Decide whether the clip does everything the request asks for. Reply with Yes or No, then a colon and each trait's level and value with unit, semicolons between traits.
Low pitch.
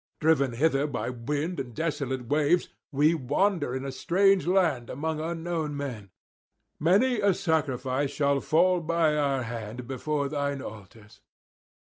No: medium, 145 Hz